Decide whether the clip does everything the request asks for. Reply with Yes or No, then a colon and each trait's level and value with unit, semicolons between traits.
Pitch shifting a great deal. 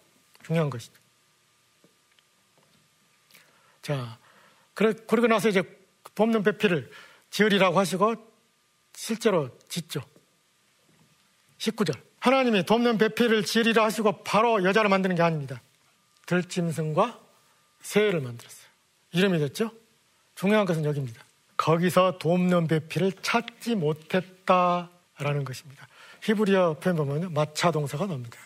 Yes: wide, 6.0 semitones